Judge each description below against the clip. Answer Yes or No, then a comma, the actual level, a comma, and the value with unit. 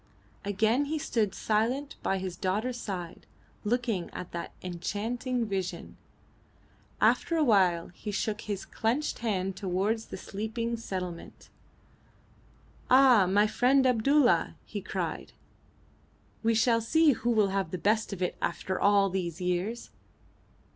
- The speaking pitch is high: Yes, high, 210 Hz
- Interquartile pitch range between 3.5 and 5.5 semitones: Yes, average, 4.0 semitones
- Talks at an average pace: No, slow, 130 wpm